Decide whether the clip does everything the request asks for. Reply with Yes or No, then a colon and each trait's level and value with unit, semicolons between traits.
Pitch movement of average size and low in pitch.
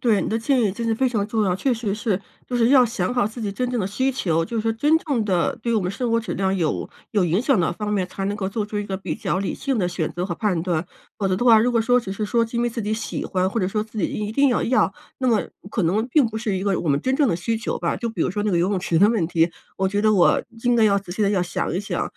No: average, 3.6 semitones; high, 210 Hz